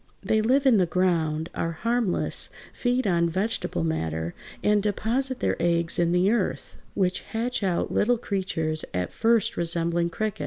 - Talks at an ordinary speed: Yes, average, 155 wpm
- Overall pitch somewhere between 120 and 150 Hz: No, medium, 185 Hz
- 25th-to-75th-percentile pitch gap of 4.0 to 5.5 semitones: Yes, average, 5.0 semitones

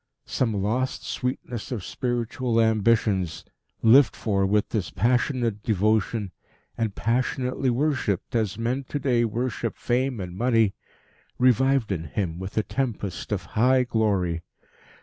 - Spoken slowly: Yes, slow, 130 wpm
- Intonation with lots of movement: No, average, 3.7 semitones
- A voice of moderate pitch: No, low, 115 Hz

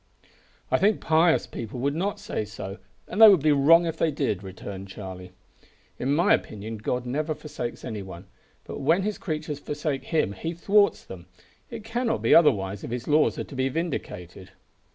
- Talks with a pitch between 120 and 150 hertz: Yes, medium, 140 Hz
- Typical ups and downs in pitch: No, wide, 8.1 semitones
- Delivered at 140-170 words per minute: No, average, 185 wpm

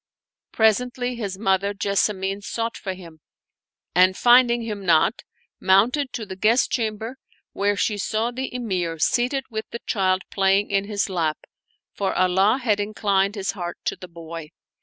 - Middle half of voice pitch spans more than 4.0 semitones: No, average, 3.3 semitones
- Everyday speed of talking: Yes, average, 160 wpm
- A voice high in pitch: Yes, high, 200 Hz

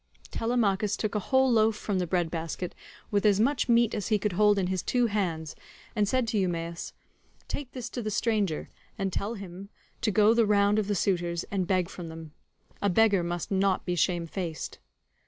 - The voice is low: No, high, 200 Hz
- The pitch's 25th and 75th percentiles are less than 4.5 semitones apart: Yes, average, 3.5 semitones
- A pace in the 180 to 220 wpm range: Yes, average, 195 wpm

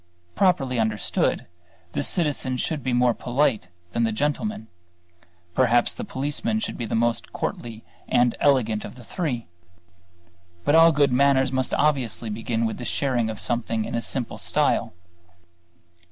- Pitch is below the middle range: Yes, low, 125 Hz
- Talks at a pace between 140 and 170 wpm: Yes, average, 150 wpm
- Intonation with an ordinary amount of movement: Yes, average, 3.7 semitones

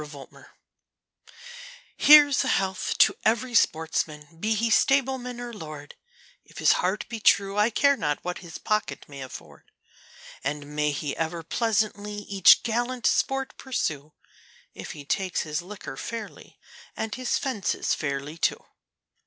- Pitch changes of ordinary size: No, wide, 7.8 semitones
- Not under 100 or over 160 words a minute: Yes, average, 145 wpm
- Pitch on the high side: Yes, high, 200 Hz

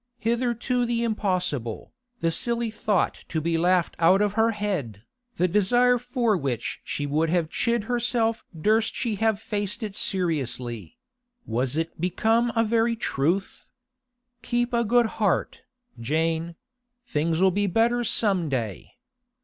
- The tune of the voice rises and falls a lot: Yes, wide, 6.1 semitones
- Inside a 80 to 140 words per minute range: Yes, slow, 135 wpm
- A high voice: Yes, high, 205 Hz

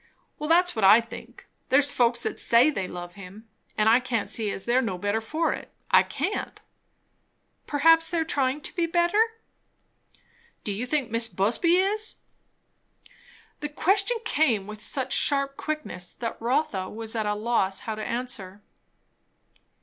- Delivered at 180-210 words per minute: No, average, 160 wpm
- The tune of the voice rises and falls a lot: Yes, wide, 6.4 semitones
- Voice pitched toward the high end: Yes, high, 240 Hz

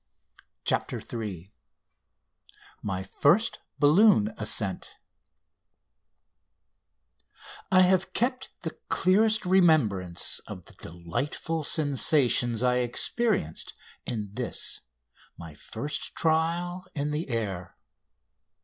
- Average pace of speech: No, slow, 85 wpm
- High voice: No, medium, 140 Hz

